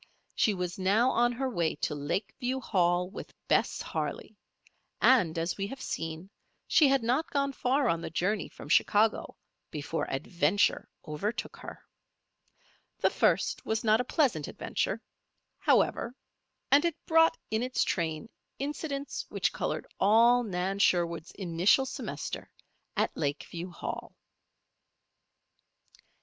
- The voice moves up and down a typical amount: No, wide, 6.9 semitones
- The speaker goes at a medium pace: No, slow, 130 wpm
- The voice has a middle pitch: No, high, 205 Hz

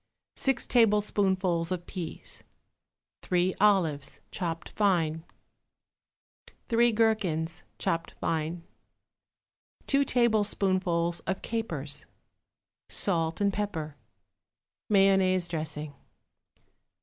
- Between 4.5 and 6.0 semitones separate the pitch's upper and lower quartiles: No, average, 3.9 semitones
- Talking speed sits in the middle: No, slow, 75 wpm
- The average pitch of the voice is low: No, medium, 185 Hz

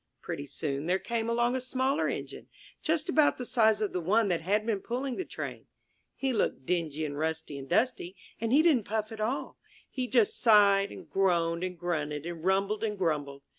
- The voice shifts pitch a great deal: Yes, wide, 6.1 semitones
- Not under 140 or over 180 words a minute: No, average, 200 wpm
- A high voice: Yes, high, 200 Hz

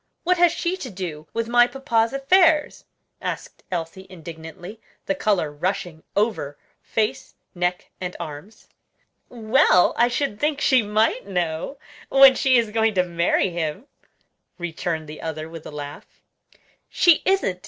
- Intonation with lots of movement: Yes, wide, 7.3 semitones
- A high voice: Yes, high, 200 Hz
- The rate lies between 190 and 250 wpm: No, average, 145 wpm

